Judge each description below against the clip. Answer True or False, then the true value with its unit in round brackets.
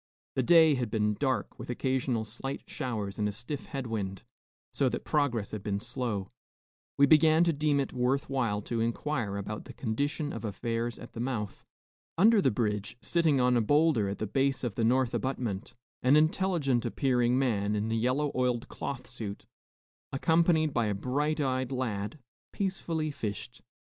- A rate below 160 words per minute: False (175 wpm)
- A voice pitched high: False (125 Hz)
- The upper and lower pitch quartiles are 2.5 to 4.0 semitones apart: False (4.5 semitones)